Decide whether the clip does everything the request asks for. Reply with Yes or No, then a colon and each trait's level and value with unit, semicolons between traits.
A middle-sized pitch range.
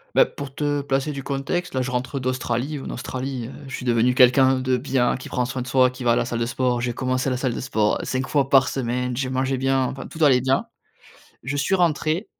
No: narrow, 1.5 semitones